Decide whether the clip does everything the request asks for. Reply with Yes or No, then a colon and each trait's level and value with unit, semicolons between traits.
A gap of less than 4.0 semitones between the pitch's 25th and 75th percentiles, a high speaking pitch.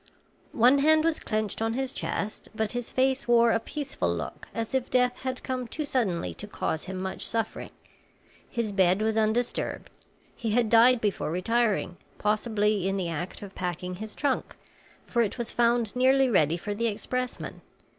Yes: average, 3.6 semitones; high, 225 Hz